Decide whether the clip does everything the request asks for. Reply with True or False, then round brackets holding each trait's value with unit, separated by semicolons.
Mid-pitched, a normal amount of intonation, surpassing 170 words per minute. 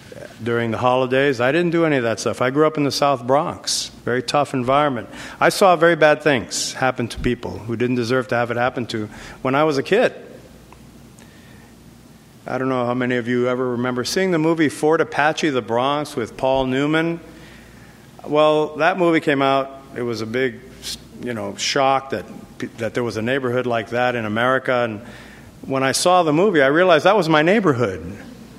False (130 Hz; 3.3 semitones; 195 wpm)